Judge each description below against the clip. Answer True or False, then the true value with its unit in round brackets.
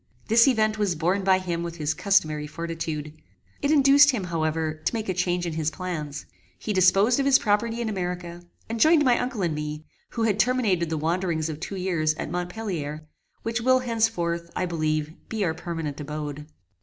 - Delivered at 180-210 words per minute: True (190 wpm)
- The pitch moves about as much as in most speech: False (5.7 semitones)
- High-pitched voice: False (180 Hz)